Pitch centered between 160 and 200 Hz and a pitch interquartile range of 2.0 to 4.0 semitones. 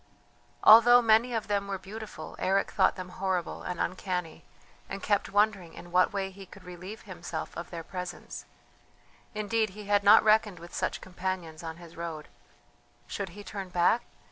Yes: high, 190 Hz; average, 2.9 semitones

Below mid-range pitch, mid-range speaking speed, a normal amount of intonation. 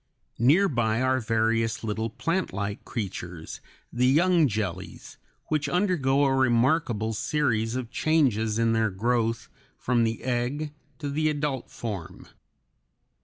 No: low, 120 Hz; slow, 120 wpm; average, 4.3 semitones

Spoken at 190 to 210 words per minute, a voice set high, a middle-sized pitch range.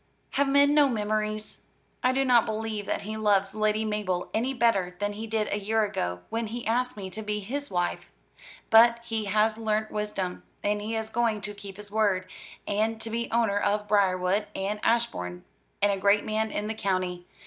No: average, 195 wpm; high, 215 Hz; narrow, 1.8 semitones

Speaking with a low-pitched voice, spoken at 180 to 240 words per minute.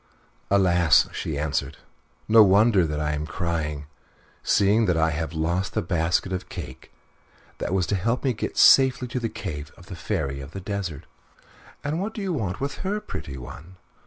Yes: very low, 90 Hz; average, 190 wpm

